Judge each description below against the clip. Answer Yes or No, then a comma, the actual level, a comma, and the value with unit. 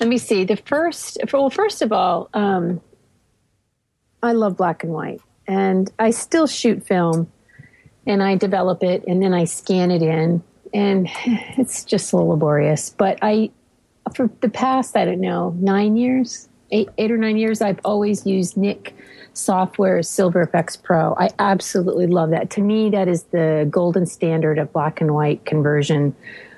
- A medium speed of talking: Yes, average, 170 wpm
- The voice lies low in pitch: No, high, 190 Hz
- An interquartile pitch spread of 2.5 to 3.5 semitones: No, average, 4.3 semitones